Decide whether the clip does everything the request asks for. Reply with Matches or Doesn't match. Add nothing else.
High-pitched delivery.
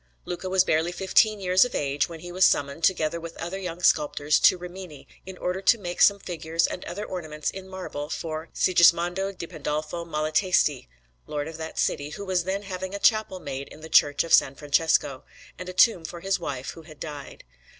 Doesn't match